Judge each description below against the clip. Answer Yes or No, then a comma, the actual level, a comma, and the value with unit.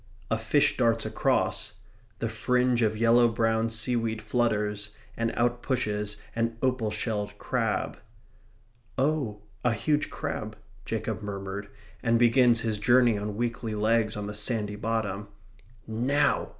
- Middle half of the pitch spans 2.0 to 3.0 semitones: Yes, narrow, 2.4 semitones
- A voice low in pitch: Yes, low, 115 Hz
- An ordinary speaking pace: No, slow, 130 wpm